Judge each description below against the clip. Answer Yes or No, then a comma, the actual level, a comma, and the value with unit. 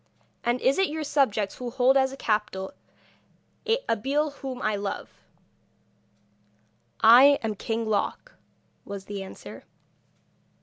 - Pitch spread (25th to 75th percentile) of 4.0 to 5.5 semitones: Yes, average, 4.5 semitones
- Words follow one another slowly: Yes, slow, 120 wpm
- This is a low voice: No, high, 235 Hz